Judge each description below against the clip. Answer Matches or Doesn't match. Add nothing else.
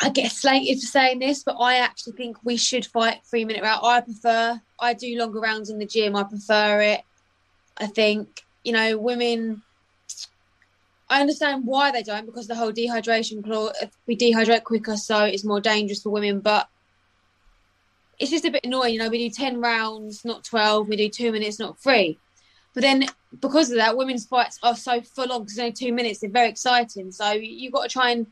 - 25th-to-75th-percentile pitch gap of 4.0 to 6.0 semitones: Doesn't match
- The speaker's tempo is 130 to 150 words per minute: Doesn't match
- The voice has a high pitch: Matches